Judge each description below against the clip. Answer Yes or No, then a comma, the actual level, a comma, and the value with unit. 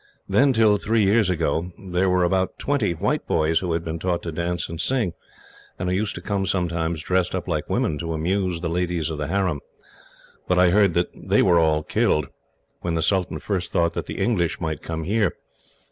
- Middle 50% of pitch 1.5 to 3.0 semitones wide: Yes, narrow, 2.6 semitones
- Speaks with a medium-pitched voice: No, very low, 90 Hz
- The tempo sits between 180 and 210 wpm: Yes, fast, 205 wpm